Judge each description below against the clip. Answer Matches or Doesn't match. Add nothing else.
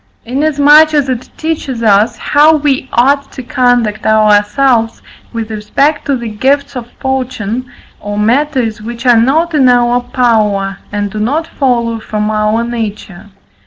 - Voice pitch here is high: Matches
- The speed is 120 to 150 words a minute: Matches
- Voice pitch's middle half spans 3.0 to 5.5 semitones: Matches